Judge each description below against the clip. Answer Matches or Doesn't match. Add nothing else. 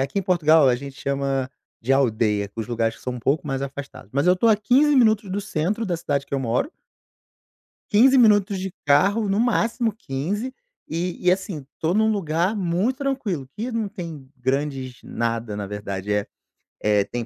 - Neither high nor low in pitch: Matches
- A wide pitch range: Matches